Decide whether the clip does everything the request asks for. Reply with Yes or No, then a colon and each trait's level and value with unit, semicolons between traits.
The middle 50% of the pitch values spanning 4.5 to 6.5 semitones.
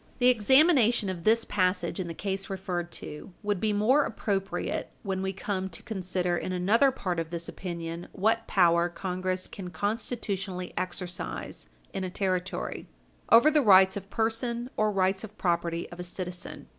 No: average, 3.2 semitones